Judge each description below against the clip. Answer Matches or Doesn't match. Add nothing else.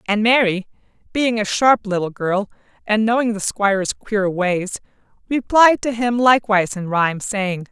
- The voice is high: Matches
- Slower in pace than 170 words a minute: Matches